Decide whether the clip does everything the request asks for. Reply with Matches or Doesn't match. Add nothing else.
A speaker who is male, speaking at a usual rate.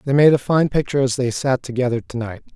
Doesn't match